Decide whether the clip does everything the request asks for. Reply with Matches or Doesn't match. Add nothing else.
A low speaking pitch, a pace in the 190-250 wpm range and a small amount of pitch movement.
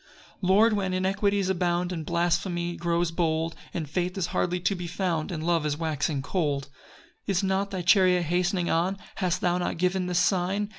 Doesn't match